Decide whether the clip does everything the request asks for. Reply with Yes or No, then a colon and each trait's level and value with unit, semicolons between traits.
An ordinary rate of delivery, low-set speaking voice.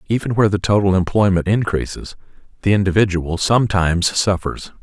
No: slow, 125 wpm; low, 100 Hz